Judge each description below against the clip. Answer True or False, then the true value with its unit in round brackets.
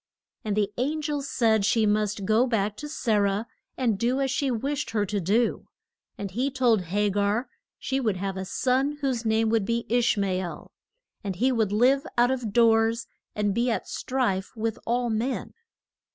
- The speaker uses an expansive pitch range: False (3.5 semitones)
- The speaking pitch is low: False (225 Hz)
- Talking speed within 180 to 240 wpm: True (195 wpm)